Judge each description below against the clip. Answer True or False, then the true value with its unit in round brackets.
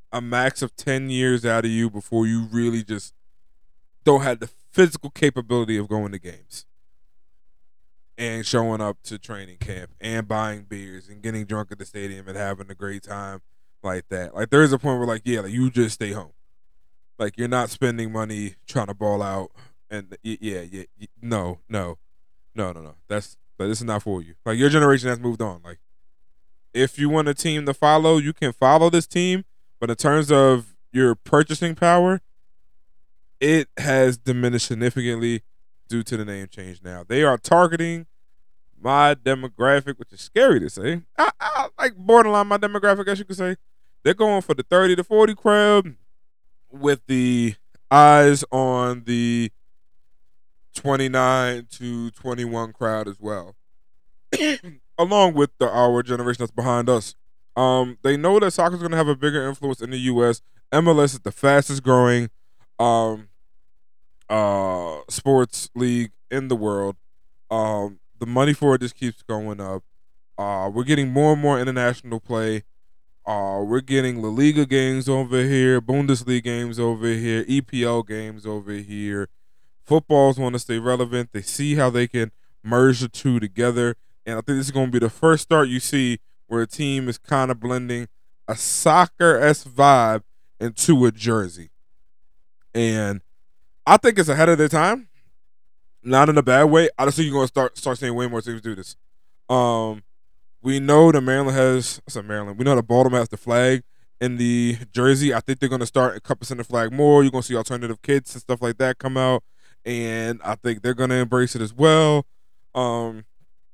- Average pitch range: True (4.4 semitones)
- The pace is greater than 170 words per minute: True (180 wpm)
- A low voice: True (120 Hz)